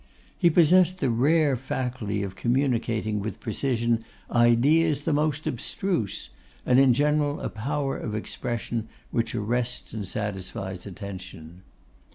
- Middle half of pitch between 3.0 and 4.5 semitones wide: No, average, 5.1 semitones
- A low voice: Yes, low, 120 Hz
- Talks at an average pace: No, slow, 125 wpm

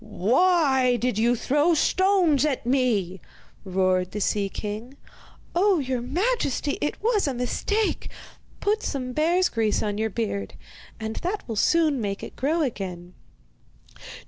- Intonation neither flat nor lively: No, wide, 7.7 semitones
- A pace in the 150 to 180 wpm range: No, average, 140 wpm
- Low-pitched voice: No, very high, 255 Hz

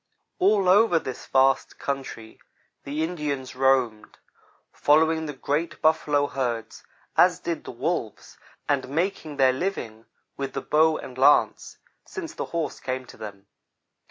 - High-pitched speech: No, medium, 145 Hz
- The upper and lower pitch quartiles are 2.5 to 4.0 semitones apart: Yes, average, 3.7 semitones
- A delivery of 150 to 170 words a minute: No, slow, 135 wpm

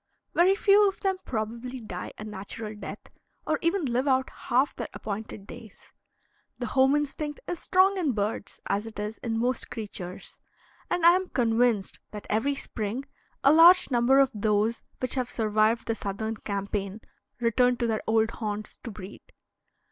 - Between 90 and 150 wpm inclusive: No, average, 165 wpm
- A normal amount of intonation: Yes, average, 4.4 semitones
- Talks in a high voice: Yes, high, 230 Hz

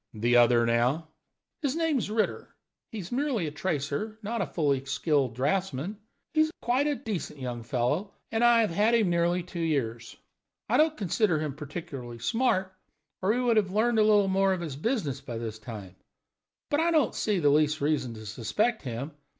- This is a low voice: No, medium, 170 Hz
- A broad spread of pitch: Yes, wide, 8.9 semitones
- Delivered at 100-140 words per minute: No, average, 185 wpm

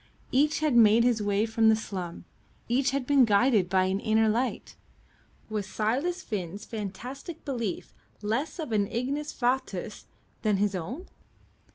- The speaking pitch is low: No, high, 225 Hz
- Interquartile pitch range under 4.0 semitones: No, average, 4.3 semitones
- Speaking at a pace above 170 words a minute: No, average, 150 wpm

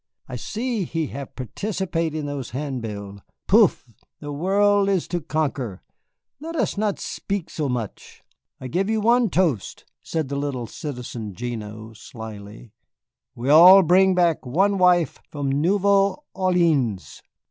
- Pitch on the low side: No, medium, 155 Hz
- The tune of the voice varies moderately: No, wide, 7.5 semitones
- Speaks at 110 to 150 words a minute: Yes, slow, 135 wpm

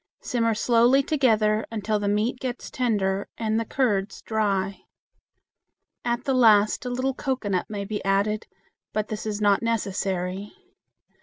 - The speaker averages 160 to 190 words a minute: No, average, 140 wpm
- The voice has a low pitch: No, high, 215 Hz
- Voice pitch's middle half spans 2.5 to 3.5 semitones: Yes, average, 2.8 semitones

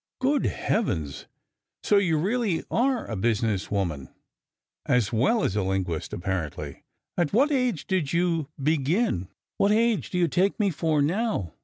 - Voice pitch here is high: No, medium, 160 Hz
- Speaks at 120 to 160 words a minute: Yes, average, 150 wpm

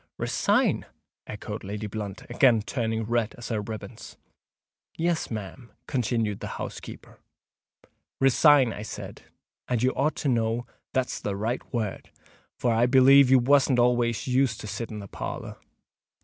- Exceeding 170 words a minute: No, average, 140 wpm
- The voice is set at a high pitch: No, low, 120 Hz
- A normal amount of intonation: Yes, average, 3.0 semitones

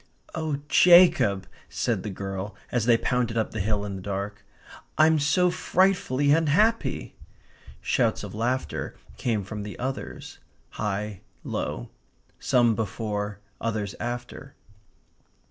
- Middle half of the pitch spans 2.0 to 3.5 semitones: No, wide, 5.6 semitones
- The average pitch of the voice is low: Yes, low, 115 Hz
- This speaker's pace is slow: Yes, slow, 120 wpm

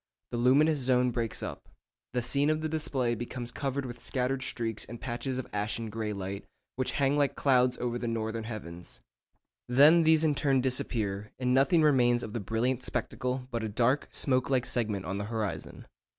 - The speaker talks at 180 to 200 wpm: Yes, average, 185 wpm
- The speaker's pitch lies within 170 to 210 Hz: No, low, 125 Hz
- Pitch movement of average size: Yes, average, 3.1 semitones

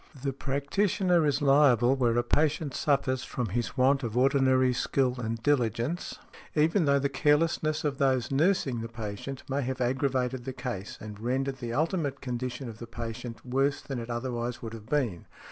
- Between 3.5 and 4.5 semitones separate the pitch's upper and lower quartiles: No, average, 2.8 semitones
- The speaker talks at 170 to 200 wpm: Yes, average, 175 wpm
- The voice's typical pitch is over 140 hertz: No, low, 130 Hz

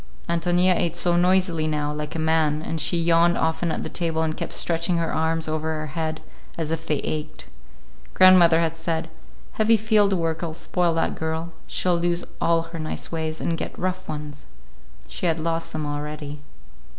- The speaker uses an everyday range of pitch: No, narrow, 1.6 semitones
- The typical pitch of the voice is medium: Yes, medium, 165 Hz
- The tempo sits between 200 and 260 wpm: No, average, 180 wpm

